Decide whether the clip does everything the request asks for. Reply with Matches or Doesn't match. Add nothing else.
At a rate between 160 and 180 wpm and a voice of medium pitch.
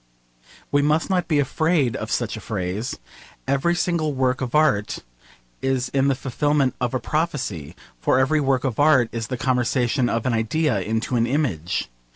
Doesn't match